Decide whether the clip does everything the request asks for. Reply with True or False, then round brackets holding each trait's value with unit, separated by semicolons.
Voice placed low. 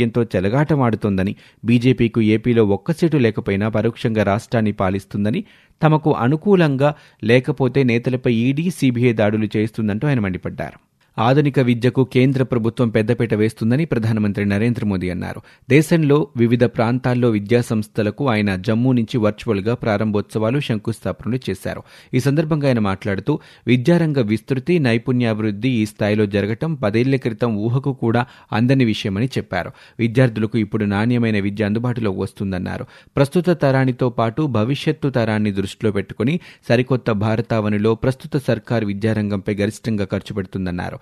True (115 Hz)